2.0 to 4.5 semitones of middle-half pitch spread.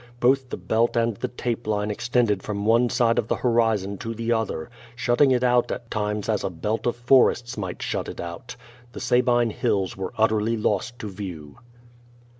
Yes: narrow, 2.6 semitones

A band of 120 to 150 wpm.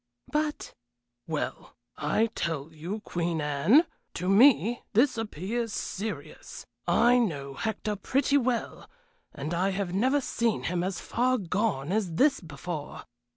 Yes: slow, 135 wpm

